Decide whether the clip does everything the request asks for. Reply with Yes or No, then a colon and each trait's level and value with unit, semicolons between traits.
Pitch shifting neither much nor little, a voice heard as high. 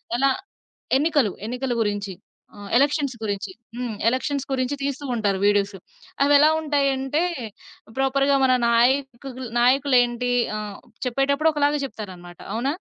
Yes: average, 3.3 semitones; very high, 260 Hz